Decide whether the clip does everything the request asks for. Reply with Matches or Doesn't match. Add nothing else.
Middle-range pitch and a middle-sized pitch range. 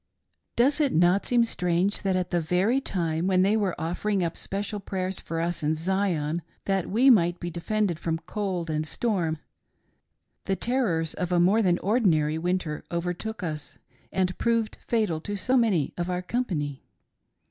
Matches